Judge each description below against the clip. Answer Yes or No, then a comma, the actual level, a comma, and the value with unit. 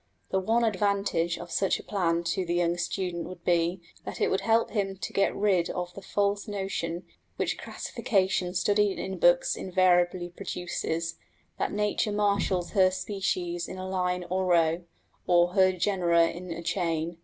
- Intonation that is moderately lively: No, narrow, 2.3 semitones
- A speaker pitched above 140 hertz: Yes, medium, 185 Hz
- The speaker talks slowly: No, average, 165 wpm